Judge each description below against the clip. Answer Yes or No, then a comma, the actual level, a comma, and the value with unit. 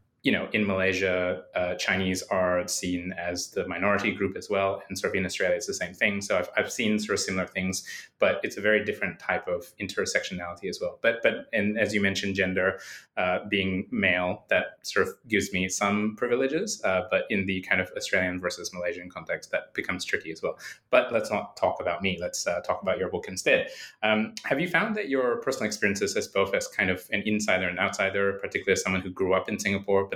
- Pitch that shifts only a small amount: Yes, narrow, 2.2 semitones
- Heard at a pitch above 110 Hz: No, very low, 95 Hz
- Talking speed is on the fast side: Yes, fast, 225 wpm